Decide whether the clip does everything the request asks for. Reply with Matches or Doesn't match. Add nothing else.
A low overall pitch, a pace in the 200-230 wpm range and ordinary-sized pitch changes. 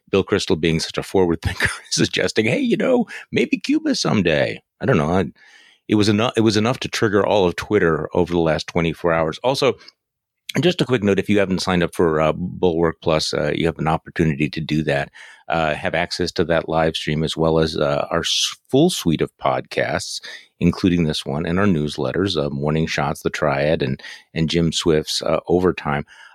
Matches